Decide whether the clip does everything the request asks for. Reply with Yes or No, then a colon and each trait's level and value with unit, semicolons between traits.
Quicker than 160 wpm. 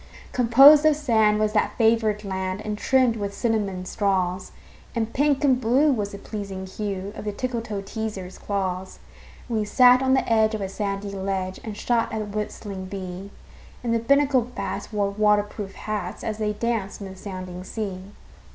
Yes: average, 180 wpm